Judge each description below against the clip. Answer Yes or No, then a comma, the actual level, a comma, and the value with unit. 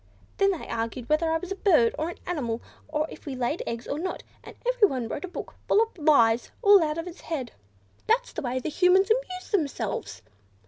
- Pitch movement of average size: No, wide, 7.1 semitones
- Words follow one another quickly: Yes, fast, 210 wpm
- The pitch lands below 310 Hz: No, very high, 320 Hz